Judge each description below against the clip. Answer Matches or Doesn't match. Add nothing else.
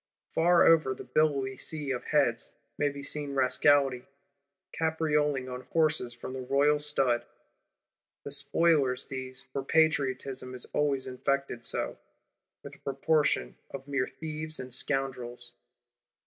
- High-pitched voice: Doesn't match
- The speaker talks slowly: Matches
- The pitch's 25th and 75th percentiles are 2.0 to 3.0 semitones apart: Matches